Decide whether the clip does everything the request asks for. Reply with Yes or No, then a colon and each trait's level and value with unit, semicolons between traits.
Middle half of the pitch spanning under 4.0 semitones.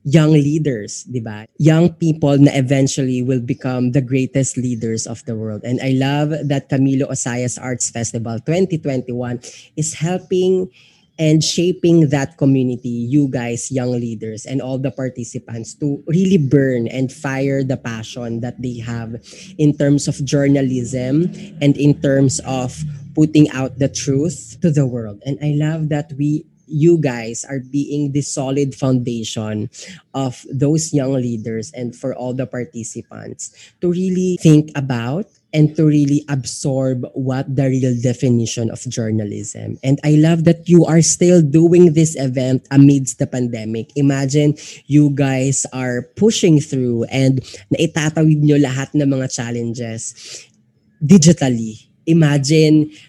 Yes: average, 3.5 semitones